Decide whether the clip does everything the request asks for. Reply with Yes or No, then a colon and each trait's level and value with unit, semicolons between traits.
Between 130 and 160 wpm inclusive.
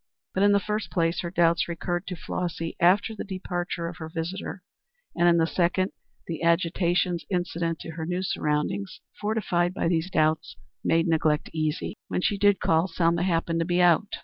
No: average, 180 wpm